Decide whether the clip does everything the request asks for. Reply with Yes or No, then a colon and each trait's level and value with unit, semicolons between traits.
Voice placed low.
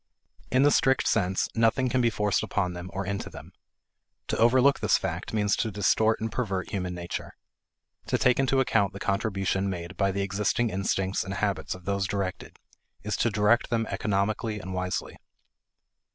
Yes: low, 100 Hz